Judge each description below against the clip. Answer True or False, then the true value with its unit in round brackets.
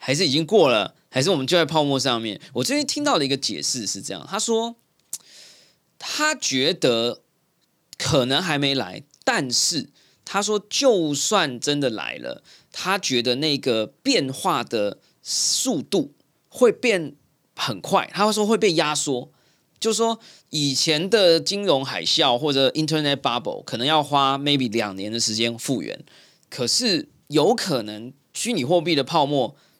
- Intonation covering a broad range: True (7.1 semitones)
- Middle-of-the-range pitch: True (150 Hz)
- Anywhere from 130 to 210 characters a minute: False (250 characters per minute)